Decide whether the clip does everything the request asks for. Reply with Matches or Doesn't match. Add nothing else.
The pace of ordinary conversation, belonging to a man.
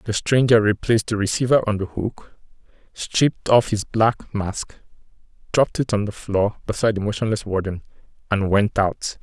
Matches